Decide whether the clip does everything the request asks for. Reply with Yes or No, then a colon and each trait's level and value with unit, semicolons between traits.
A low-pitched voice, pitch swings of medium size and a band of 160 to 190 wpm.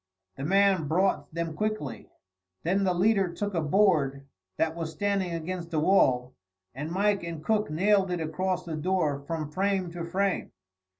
No: medium, 175 Hz; average, 3.8 semitones; average, 165 wpm